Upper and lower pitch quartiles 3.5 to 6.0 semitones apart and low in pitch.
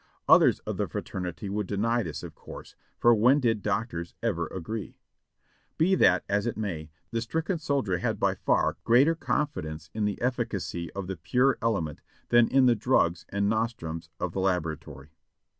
Yes: wide, 5.5 semitones; low, 105 Hz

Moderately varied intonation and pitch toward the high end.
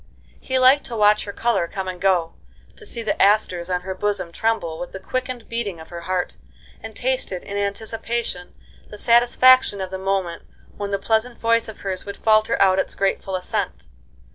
Yes: average, 3.7 semitones; high, 200 Hz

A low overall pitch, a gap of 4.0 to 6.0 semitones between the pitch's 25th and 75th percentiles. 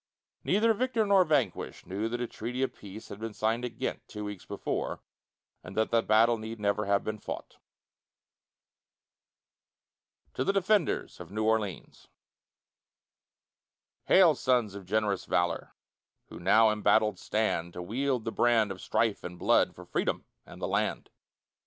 No: low, 110 Hz; average, 3.4 semitones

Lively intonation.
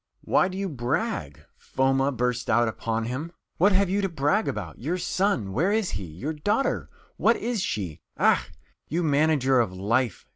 Yes: wide, 8.4 semitones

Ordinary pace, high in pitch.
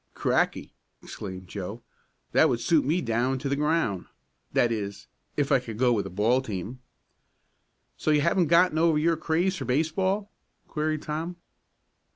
No: average, 160 wpm; medium, 145 Hz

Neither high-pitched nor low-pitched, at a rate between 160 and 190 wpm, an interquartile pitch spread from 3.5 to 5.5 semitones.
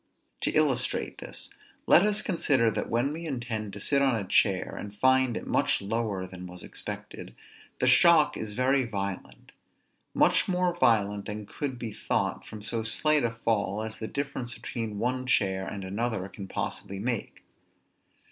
No: low, 115 Hz; average, 165 wpm; average, 4.4 semitones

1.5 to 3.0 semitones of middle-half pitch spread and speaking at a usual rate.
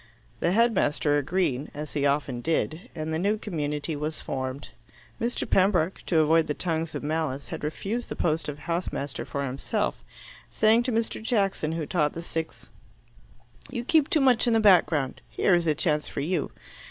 No: average, 5.0 semitones; average, 180 wpm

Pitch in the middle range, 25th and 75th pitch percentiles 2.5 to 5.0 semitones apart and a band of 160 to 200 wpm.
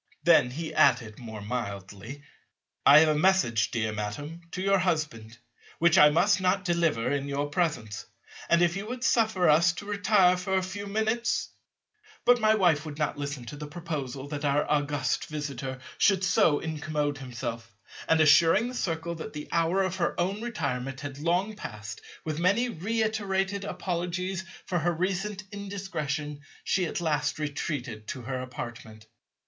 No: medium, 160 Hz; wide, 5.4 semitones; average, 165 wpm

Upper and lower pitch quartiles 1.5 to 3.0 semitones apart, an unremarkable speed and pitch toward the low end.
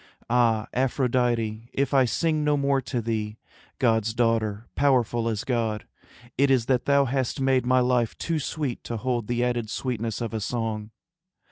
Yes: average, 2.7 semitones; average, 165 wpm; low, 120 Hz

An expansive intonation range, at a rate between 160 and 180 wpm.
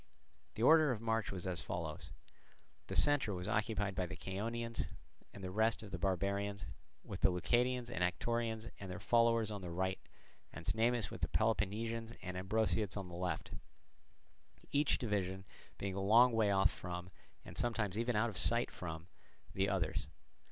No: average, 3.7 semitones; average, 170 wpm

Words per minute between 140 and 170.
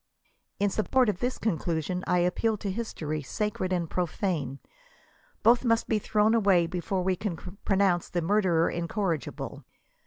Yes: average, 145 wpm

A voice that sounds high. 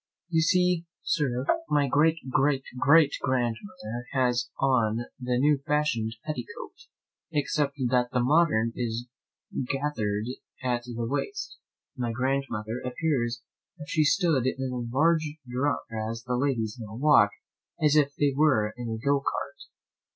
No: low, 130 Hz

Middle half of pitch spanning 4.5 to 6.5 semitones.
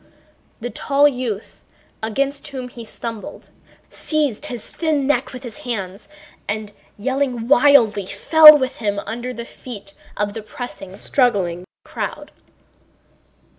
Yes: average, 4.8 semitones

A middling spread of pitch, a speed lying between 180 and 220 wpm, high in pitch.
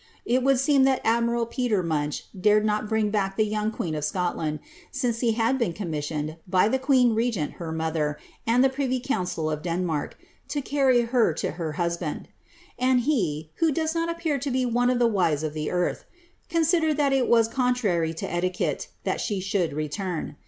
No: wide, 7.2 semitones; average, 190 wpm; high, 215 Hz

